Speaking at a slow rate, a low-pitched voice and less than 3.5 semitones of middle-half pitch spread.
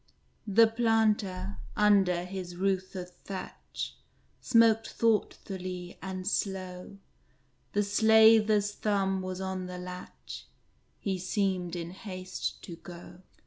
No: slow, 105 wpm; high, 190 Hz; narrow, 2.4 semitones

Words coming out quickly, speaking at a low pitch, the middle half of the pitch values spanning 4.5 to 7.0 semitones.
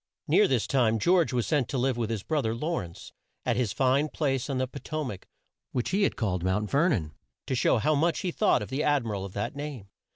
Yes: fast, 260 wpm; low, 130 Hz; average, 5.2 semitones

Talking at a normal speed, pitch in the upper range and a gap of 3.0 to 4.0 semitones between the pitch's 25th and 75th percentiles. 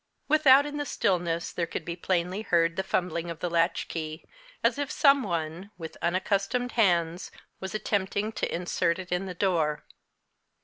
No: average, 165 wpm; medium, 180 Hz; average, 3.3 semitones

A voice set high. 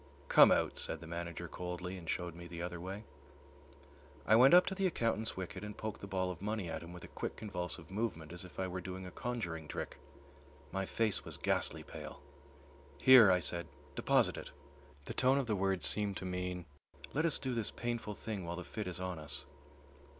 No: very low, 95 Hz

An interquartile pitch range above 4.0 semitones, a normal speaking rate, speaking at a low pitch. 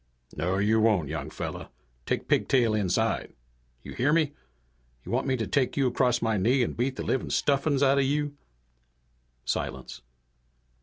Yes: average, 4.5 semitones; average, 160 wpm; low, 120 Hz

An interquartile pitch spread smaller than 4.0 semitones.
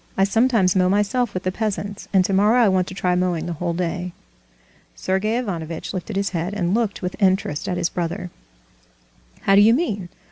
Yes: narrow, 2.5 semitones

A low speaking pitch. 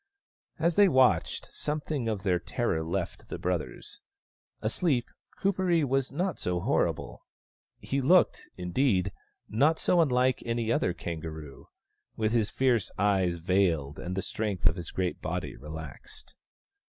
Yes: low, 110 Hz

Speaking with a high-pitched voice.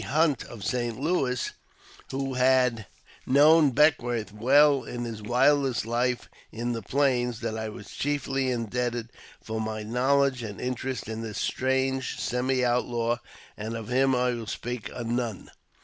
No: low, 125 Hz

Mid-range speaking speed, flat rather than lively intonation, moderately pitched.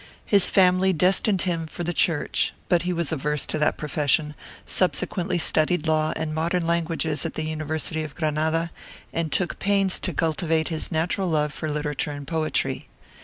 Yes: average, 170 wpm; narrow, 2.2 semitones; medium, 160 Hz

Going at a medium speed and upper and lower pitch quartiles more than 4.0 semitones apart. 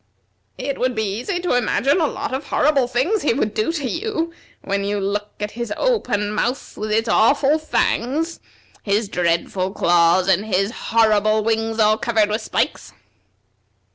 Yes: average, 165 wpm; average, 4.8 semitones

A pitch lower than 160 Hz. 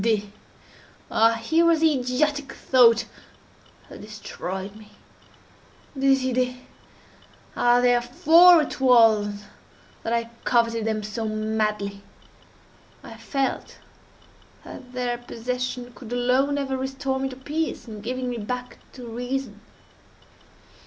No: high, 245 Hz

